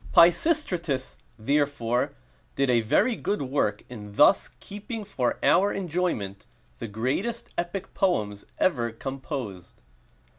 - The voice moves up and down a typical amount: No, wide, 8.2 semitones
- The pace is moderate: No, slow, 110 wpm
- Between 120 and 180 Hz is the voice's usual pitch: Yes, medium, 140 Hz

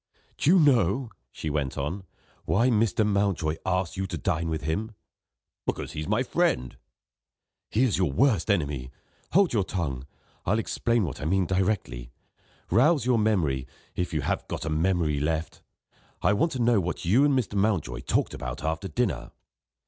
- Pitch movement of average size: No, wide, 6.1 semitones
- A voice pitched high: No, very low, 95 Hz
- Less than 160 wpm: No, average, 170 wpm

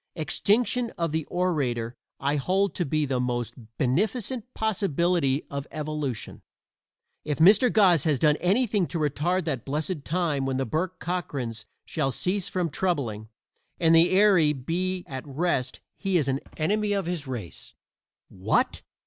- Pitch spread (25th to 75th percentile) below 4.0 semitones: No, average, 5.2 semitones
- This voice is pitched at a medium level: Yes, medium, 160 Hz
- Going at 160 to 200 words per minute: No, average, 150 wpm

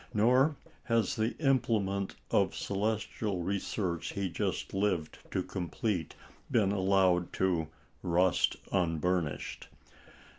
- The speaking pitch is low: Yes, very low, 95 Hz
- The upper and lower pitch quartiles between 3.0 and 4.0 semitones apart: Yes, average, 3.4 semitones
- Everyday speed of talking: No, slow, 100 wpm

